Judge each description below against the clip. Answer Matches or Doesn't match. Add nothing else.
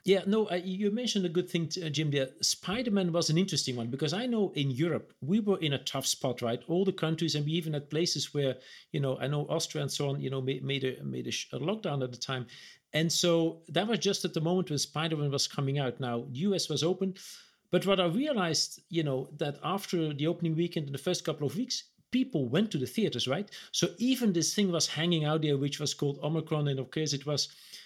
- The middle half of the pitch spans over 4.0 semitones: Matches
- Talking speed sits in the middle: Doesn't match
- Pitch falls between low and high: Matches